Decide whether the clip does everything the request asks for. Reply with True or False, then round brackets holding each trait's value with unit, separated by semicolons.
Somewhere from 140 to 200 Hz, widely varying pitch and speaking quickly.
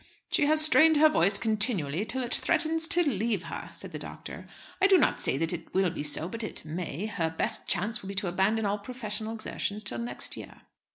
False (210 Hz; 5.8 semitones; 220 wpm)